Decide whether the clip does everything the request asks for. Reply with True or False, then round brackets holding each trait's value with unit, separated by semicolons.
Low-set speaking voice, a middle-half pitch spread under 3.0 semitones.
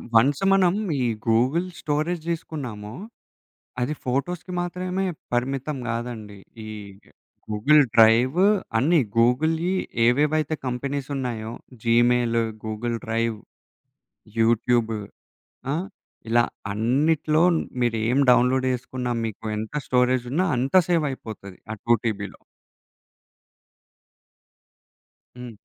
False (125 Hz; 4.6 semitones)